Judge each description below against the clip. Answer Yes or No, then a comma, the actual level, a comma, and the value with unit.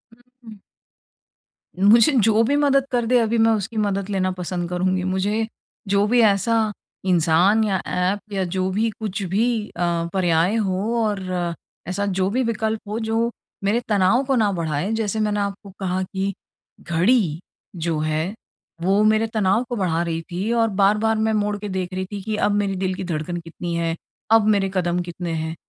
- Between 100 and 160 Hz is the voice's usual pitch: No, high, 200 Hz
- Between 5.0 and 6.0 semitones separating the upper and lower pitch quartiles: No, average, 3.2 semitones